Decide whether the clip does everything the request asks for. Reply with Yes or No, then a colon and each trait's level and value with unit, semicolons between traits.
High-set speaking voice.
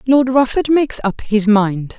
Yes: high, 235 Hz